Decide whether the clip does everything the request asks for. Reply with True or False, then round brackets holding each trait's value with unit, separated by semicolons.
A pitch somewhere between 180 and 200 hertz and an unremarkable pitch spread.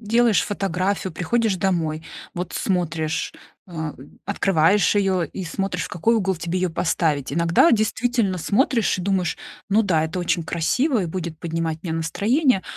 True (185 Hz; 3.7 semitones)